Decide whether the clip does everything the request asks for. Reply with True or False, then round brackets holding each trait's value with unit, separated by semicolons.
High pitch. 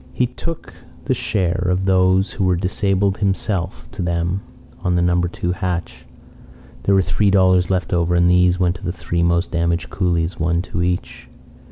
False (90 Hz)